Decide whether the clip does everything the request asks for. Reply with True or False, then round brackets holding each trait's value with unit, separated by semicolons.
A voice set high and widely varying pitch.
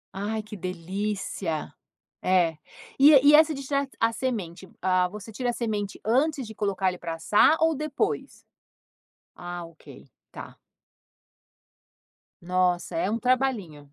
True (210 Hz; 6.1 semitones)